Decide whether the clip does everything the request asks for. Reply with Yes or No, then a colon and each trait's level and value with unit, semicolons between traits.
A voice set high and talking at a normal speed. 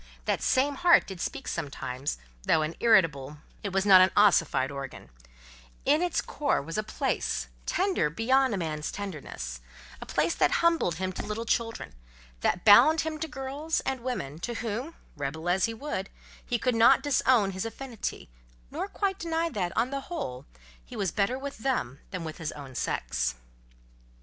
Yes: high, 205 Hz; average, 175 wpm